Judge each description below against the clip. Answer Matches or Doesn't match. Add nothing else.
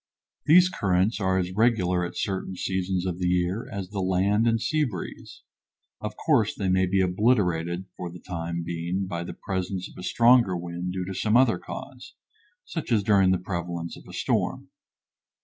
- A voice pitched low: Matches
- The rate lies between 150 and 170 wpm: Doesn't match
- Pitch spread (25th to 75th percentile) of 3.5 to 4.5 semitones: Doesn't match